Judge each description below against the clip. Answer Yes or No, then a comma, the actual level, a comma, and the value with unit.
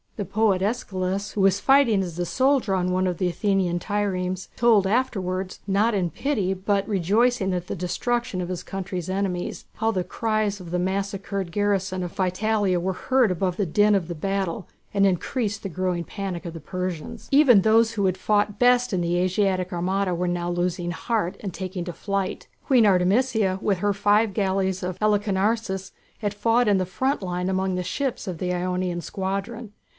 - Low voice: No, high, 195 Hz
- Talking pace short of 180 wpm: No, average, 185 wpm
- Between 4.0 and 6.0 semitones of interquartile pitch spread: No, narrow, 2.4 semitones